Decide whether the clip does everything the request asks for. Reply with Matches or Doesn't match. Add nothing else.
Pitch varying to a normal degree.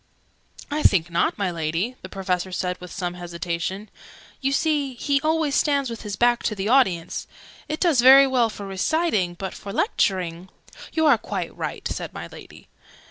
Doesn't match